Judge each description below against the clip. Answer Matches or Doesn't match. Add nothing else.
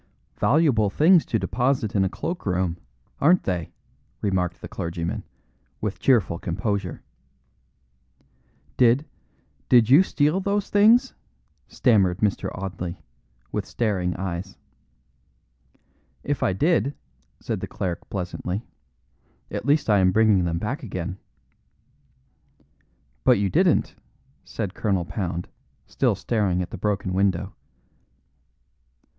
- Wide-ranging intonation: Matches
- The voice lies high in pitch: Doesn't match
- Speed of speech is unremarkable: Doesn't match